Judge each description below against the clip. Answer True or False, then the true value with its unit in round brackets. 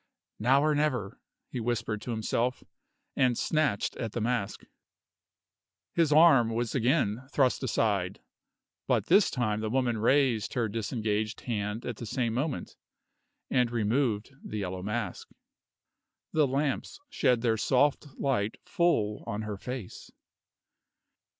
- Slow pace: True (130 wpm)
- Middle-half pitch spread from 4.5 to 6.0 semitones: False (3.8 semitones)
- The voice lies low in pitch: True (120 Hz)